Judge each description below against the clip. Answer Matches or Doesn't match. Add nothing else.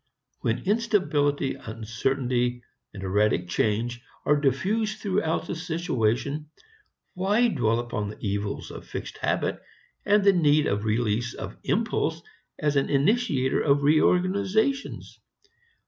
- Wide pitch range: Matches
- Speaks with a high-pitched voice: Doesn't match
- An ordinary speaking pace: Doesn't match